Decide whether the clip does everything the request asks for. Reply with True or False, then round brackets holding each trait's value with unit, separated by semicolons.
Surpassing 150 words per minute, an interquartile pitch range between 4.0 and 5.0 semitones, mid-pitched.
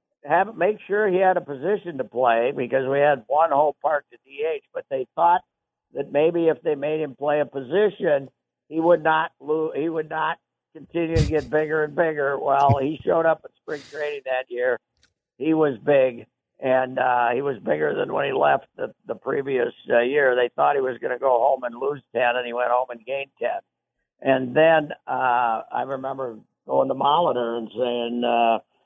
True (200 wpm; 4.3 semitones; 145 Hz)